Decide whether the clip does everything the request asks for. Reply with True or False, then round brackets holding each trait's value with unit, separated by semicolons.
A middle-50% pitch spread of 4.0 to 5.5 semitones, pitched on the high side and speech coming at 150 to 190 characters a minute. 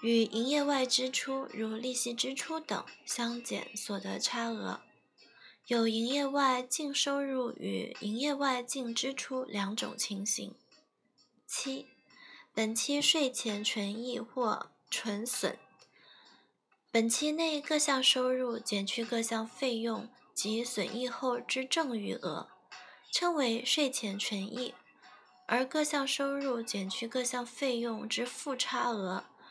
False (2.9 semitones; 245 Hz; 180 characters per minute)